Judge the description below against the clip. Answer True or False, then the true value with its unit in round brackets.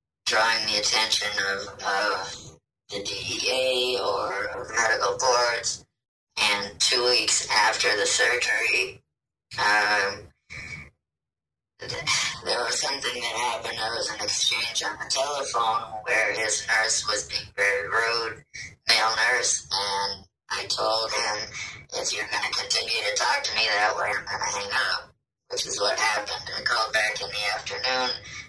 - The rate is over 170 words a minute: False (150 wpm)